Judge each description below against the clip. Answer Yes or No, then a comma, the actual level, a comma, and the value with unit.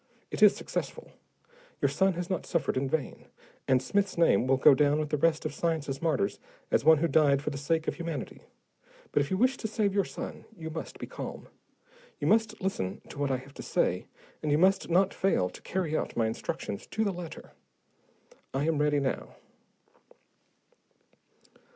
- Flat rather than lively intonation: No, average, 4.8 semitones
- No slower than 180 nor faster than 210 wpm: Yes, average, 190 wpm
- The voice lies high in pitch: No, medium, 155 Hz